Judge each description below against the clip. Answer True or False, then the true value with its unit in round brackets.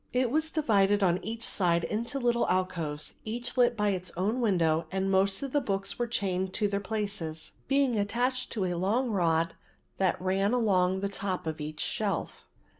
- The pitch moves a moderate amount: True (4.2 semitones)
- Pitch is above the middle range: True (200 Hz)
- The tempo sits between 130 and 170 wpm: False (185 wpm)